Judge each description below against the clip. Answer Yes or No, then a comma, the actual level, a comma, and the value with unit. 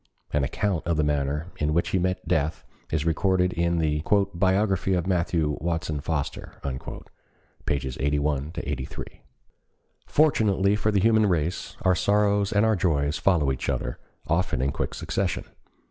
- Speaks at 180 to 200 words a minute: No, average, 145 wpm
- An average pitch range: Yes, average, 4.5 semitones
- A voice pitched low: Yes, very low, 85 Hz